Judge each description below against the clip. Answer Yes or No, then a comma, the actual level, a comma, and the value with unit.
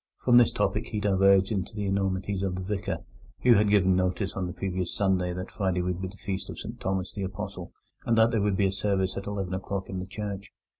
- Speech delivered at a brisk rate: Yes, fast, 235 wpm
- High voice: No, very low, 95 Hz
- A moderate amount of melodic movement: No, narrow, 1.6 semitones